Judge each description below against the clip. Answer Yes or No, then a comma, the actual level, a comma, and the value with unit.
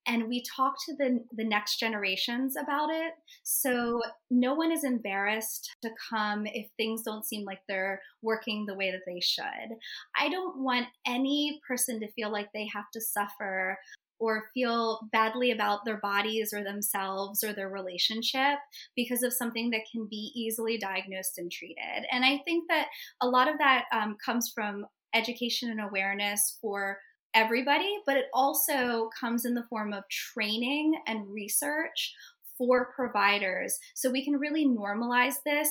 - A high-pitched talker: Yes, high, 230 Hz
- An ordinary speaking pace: Yes, average, 165 wpm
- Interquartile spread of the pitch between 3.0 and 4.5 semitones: Yes, average, 3.9 semitones